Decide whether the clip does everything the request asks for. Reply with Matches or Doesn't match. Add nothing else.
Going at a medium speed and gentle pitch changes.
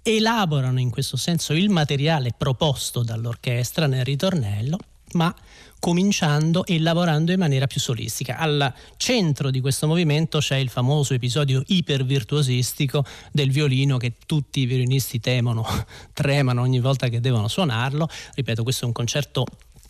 Doesn't match